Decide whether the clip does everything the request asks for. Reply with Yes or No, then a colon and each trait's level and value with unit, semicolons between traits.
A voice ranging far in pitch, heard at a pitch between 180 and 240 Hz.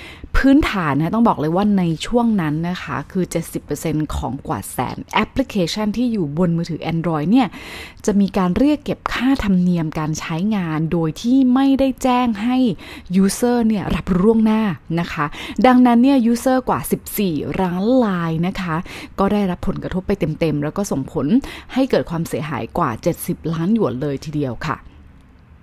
Yes: wide, 6.3 semitones; medium, 185 Hz